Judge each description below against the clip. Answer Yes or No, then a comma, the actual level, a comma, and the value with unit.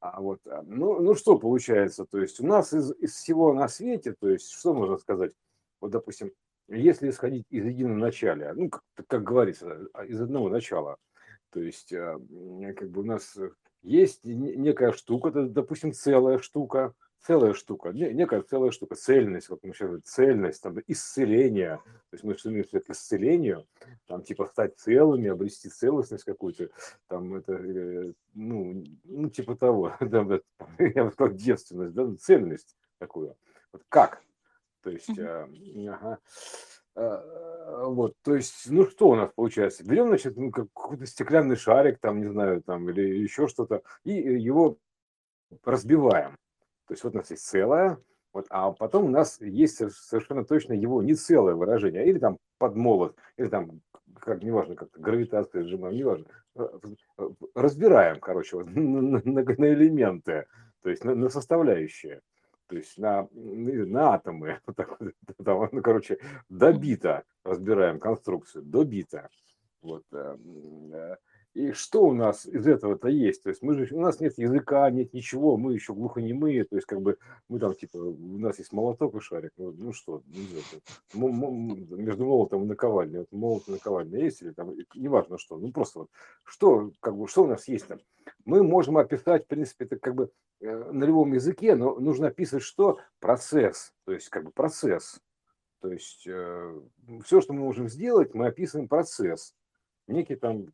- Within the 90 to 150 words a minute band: No, fast, 160 wpm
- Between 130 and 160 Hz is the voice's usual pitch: Yes, low, 135 Hz